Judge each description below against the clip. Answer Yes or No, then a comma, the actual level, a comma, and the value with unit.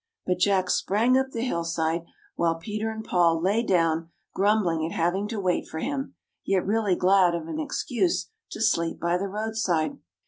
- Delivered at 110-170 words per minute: No, average, 180 wpm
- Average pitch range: Yes, average, 4.6 semitones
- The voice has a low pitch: No, high, 190 Hz